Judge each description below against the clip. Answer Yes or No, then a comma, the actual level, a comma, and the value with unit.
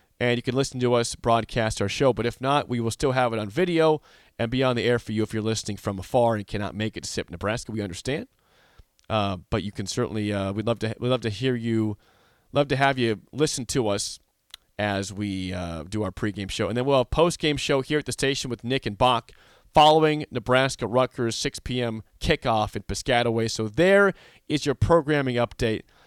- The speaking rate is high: Yes, fast, 225 wpm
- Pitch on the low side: Yes, low, 115 Hz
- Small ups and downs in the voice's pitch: No, average, 3.9 semitones